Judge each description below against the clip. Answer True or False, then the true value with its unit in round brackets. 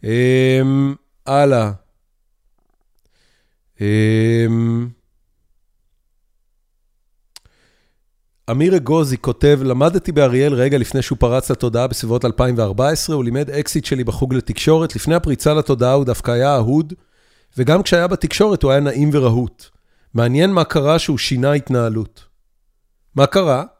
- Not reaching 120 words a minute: True (110 wpm)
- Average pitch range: True (4.0 semitones)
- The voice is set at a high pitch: False (135 Hz)